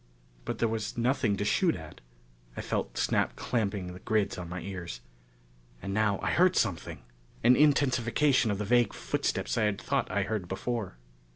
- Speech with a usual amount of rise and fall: Yes, average, 3.8 semitones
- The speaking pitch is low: Yes, low, 105 Hz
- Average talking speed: Yes, average, 175 wpm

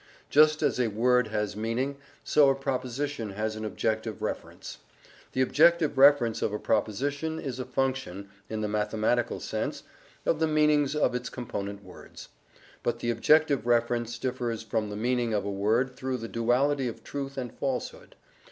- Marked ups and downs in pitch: No, average, 3.9 semitones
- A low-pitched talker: Yes, low, 125 Hz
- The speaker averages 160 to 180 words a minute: Yes, average, 165 wpm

